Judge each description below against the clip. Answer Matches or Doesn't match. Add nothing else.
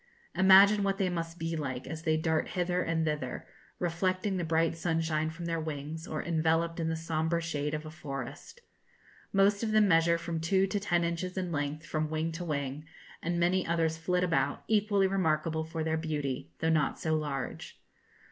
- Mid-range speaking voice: Matches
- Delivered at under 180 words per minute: Doesn't match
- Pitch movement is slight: Matches